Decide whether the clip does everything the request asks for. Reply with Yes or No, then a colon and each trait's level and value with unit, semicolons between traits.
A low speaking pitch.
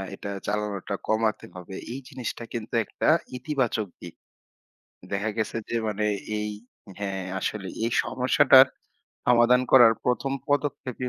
Yes: low, 110 Hz